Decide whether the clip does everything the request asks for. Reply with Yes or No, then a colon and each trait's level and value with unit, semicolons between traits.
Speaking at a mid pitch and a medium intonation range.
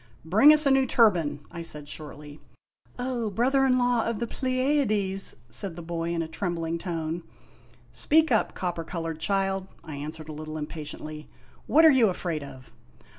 No: medium, 175 Hz; wide, 7.1 semitones